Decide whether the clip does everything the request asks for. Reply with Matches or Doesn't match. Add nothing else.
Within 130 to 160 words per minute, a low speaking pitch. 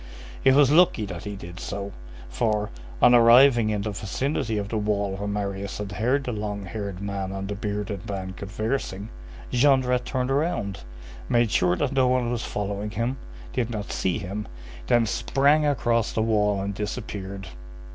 Doesn't match